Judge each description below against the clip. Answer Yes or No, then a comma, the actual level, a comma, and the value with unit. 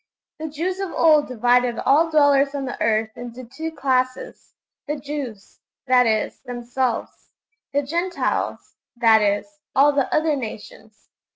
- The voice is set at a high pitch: Yes, very high, 265 Hz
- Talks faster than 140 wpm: No, slow, 135 wpm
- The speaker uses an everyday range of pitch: Yes, average, 3.8 semitones